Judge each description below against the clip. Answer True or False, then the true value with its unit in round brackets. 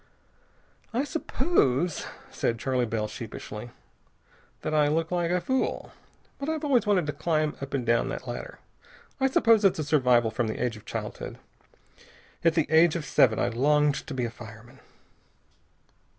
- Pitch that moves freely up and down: True (6.8 semitones)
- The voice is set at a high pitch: False (150 Hz)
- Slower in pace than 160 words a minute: False (165 wpm)